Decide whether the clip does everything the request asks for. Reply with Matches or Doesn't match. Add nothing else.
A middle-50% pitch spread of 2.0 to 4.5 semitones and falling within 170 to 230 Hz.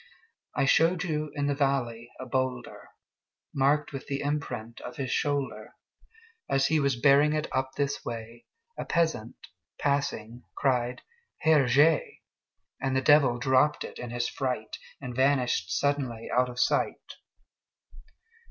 Doesn't match